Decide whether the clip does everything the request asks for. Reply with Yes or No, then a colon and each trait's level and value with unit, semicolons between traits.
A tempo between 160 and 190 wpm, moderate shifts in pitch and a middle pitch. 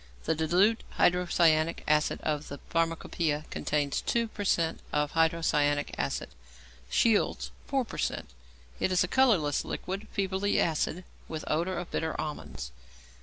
No: slow, 135 wpm; average, 3.7 semitones; medium, 165 Hz